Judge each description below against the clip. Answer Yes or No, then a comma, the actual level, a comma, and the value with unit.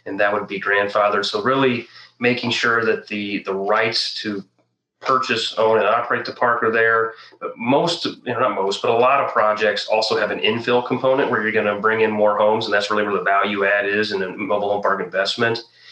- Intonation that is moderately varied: No, narrow, 2.3 semitones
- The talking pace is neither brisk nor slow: No, fast, 220 wpm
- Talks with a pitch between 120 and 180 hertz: No, low, 105 Hz